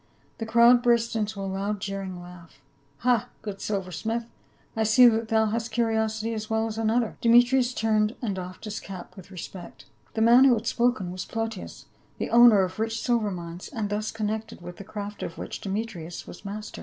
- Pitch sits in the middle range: No, high, 215 Hz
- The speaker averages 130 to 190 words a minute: No, average, 200 wpm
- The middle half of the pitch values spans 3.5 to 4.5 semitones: No, average, 2.8 semitones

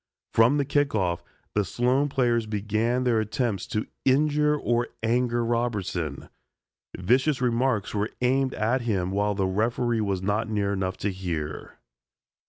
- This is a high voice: No, low, 115 Hz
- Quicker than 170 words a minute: No, average, 145 wpm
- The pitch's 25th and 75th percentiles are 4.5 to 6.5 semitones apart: No, average, 3.9 semitones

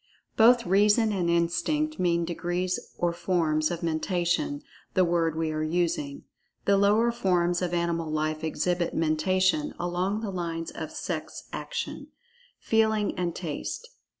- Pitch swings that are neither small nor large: Yes, average, 3.0 semitones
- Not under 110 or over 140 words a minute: Yes, slow, 135 wpm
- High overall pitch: No, medium, 175 Hz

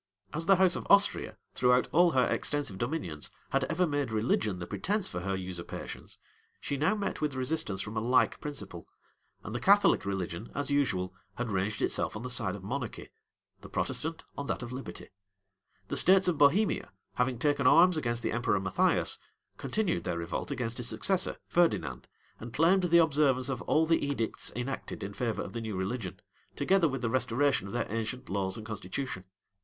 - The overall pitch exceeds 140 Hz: No, low, 125 Hz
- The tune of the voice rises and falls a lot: Yes, wide, 6.8 semitones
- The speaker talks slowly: No, average, 185 wpm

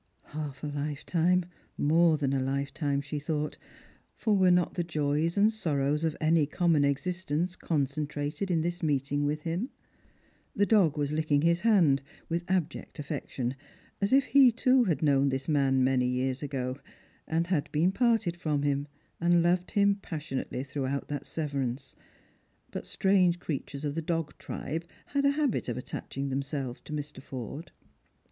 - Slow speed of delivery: No, average, 155 wpm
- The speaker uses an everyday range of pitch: Yes, average, 3.8 semitones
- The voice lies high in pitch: No, medium, 150 Hz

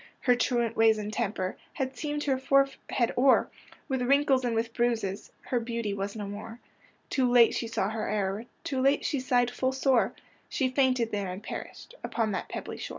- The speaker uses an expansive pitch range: No, average, 3.2 semitones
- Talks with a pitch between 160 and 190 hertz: No, high, 240 Hz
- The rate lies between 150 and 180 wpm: No, average, 190 wpm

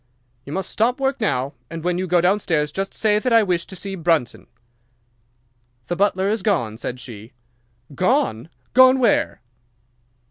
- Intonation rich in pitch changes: Yes, wide, 9.0 semitones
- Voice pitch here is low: No, medium, 170 Hz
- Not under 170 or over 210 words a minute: No, average, 155 wpm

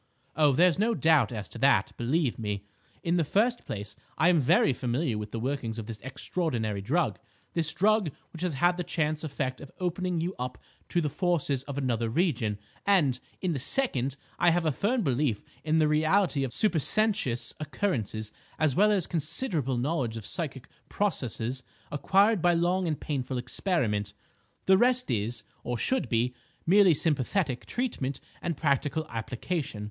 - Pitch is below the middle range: No, medium, 150 Hz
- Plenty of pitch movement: Yes, wide, 6.2 semitones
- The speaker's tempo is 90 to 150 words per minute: No, average, 165 wpm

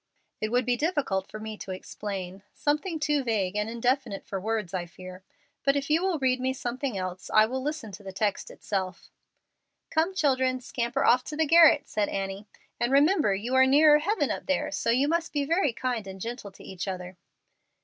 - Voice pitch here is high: Yes, high, 240 Hz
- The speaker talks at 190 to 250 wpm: Yes, average, 200 wpm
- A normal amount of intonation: No, wide, 6.6 semitones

